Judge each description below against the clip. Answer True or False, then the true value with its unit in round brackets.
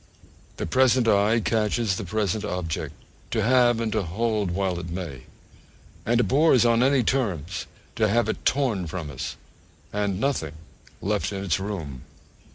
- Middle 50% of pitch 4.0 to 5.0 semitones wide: True (4.5 semitones)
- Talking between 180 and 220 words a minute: False (155 wpm)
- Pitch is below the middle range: True (105 Hz)